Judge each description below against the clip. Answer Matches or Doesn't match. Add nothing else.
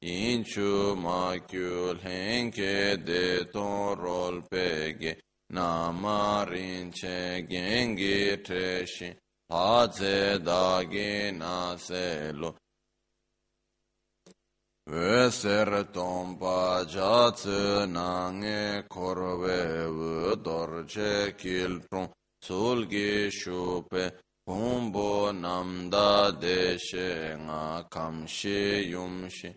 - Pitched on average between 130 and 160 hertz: Doesn't match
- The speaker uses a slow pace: Matches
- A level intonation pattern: Matches